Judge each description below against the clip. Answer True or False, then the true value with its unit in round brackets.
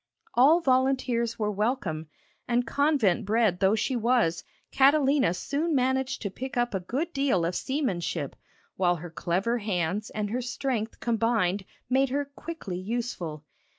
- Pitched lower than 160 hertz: False (235 Hz)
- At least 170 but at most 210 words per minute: False (145 wpm)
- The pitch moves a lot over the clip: True (5.7 semitones)